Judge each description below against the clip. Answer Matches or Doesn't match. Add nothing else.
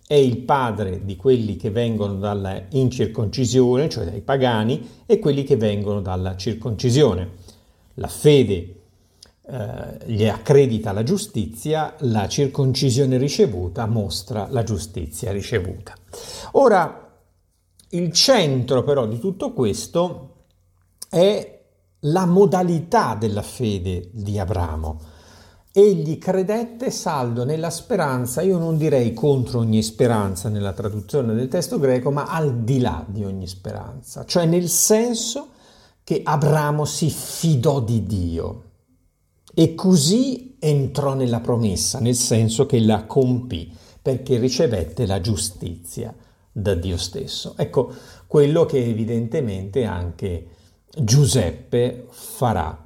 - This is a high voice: Doesn't match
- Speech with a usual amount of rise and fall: Doesn't match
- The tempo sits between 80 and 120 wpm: Matches